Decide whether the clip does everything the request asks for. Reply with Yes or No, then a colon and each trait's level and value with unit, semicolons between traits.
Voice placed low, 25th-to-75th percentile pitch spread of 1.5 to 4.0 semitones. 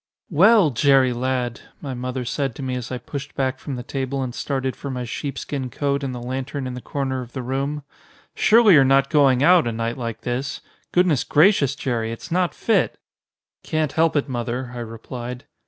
Yes: low, 130 Hz; narrow, 2.5 semitones